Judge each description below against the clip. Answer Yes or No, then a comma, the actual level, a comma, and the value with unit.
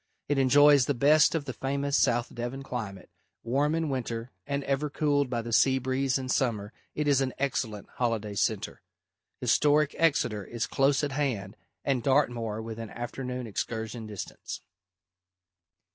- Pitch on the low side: Yes, low, 130 Hz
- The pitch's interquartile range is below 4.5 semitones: Yes, average, 3.5 semitones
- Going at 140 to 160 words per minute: Yes, average, 150 wpm